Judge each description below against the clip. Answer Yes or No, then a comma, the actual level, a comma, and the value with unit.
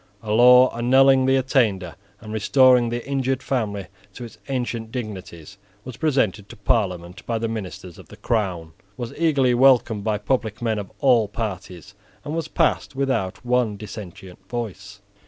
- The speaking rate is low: No, average, 155 wpm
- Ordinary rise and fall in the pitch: Yes, average, 4.2 semitones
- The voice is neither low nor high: No, low, 115 Hz